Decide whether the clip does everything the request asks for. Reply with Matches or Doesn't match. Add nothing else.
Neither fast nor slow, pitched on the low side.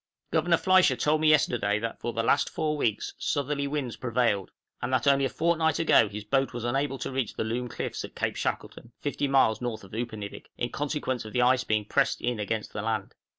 Doesn't match